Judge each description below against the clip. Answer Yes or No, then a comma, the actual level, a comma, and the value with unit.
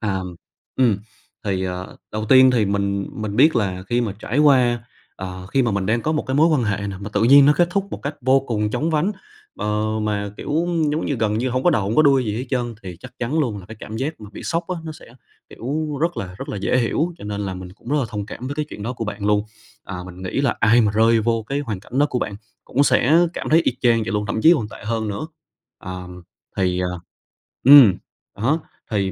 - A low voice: Yes, low, 115 Hz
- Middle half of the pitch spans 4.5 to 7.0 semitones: Yes, average, 5.3 semitones